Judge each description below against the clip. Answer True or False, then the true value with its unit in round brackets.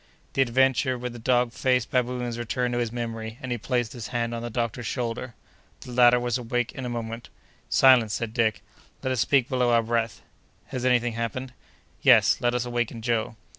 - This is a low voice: True (120 Hz)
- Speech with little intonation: True (1.3 semitones)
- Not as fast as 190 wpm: False (200 wpm)